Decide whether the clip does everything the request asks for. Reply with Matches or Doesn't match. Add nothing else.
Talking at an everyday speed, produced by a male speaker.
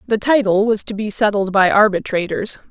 Doesn't match